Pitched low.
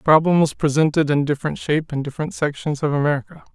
No: medium, 150 Hz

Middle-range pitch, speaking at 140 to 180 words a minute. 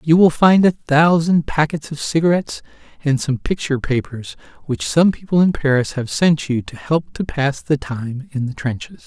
No: medium, 150 Hz; average, 190 wpm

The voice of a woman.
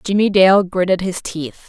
Yes: female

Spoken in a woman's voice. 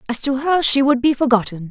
Yes: female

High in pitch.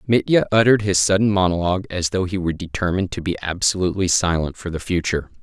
No: very low, 95 Hz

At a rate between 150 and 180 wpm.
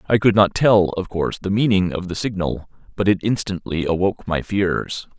No: average, 195 wpm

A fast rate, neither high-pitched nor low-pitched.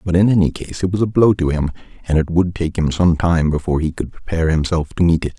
No: fast, 280 wpm; very low, 85 Hz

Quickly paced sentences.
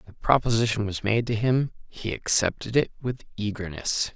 No: average, 175 wpm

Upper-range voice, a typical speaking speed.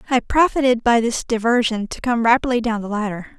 Yes: high, 235 Hz; average, 195 wpm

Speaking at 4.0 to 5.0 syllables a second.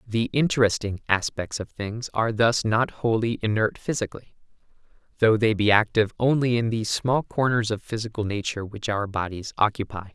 No: 5.5 syllables/s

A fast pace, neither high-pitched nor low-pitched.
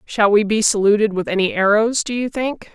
No: fast, 220 wpm; high, 215 Hz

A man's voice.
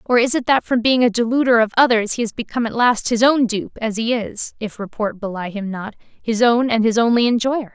No: female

